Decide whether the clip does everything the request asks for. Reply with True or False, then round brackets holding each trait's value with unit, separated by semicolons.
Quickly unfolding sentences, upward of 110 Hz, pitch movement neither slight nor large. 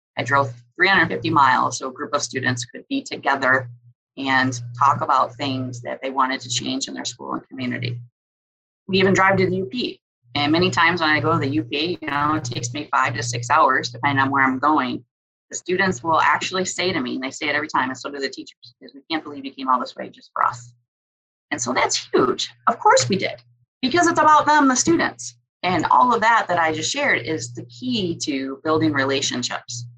True (225 wpm; 140 Hz; 5.0 semitones)